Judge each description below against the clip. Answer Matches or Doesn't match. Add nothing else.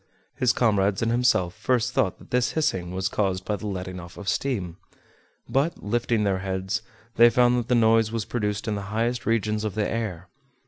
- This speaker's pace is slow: Doesn't match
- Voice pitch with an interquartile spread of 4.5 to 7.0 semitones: Doesn't match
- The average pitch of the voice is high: Doesn't match